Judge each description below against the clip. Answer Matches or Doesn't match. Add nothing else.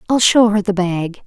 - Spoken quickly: Matches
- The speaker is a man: Doesn't match